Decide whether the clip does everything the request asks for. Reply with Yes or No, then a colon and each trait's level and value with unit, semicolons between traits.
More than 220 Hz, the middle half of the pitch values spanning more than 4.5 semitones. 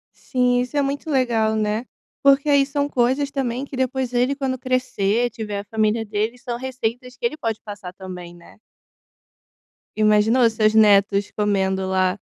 No: high, 235 Hz; average, 3.7 semitones